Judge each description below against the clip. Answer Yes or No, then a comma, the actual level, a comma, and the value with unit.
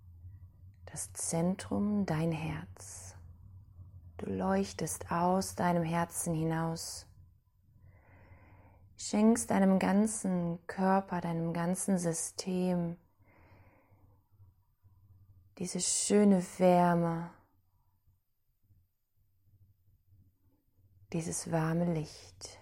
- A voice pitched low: Yes, low, 100 Hz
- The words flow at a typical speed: No, slow, 60 wpm